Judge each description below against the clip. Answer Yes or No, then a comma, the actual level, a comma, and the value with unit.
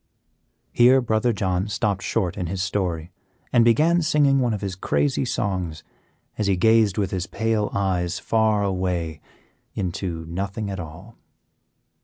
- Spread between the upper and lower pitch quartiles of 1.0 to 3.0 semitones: No, average, 3.8 semitones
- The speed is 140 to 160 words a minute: Yes, average, 150 wpm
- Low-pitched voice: Yes, low, 100 Hz